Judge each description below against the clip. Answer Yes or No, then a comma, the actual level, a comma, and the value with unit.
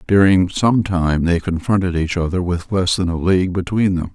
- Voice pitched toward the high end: No, very low, 90 Hz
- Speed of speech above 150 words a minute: Yes, fast, 205 wpm